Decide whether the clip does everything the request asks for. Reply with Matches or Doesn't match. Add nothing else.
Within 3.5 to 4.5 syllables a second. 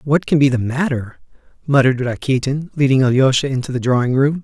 Doesn't match